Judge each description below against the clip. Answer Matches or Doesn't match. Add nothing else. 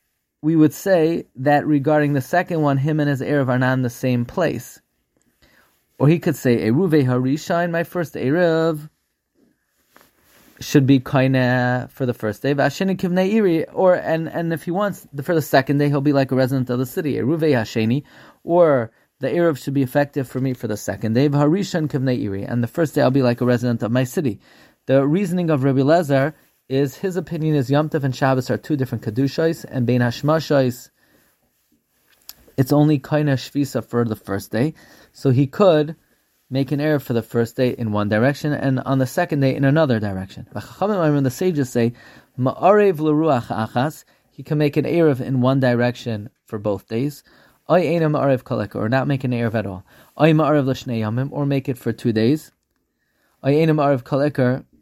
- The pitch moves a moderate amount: Matches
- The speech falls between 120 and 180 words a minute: Matches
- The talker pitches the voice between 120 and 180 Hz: Matches